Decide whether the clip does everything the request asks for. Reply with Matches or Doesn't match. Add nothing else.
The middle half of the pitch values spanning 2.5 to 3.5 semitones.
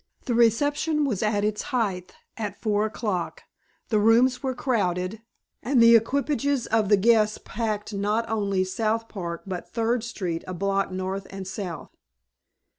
Matches